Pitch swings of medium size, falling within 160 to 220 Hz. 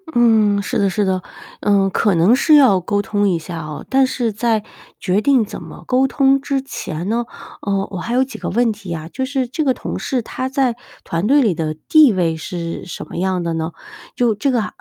No: wide, 5.8 semitones; high, 210 Hz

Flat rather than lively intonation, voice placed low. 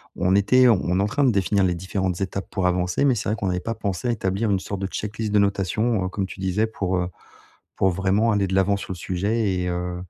Yes: narrow, 2.3 semitones; very low, 95 Hz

